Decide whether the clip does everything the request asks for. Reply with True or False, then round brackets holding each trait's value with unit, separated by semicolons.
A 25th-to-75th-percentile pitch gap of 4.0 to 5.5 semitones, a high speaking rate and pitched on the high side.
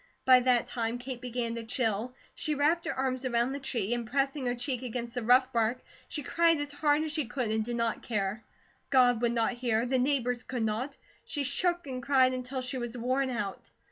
False (2.5 semitones; 215 wpm; 250 Hz)